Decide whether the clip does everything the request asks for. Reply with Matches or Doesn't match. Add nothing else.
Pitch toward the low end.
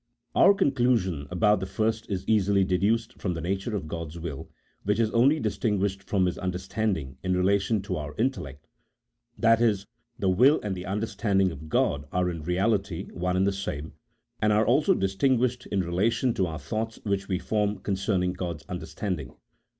Matches